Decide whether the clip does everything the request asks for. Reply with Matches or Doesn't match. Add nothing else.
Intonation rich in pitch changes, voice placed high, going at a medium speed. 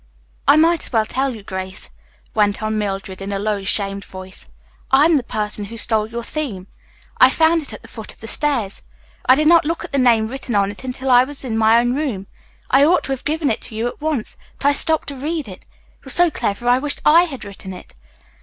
Doesn't match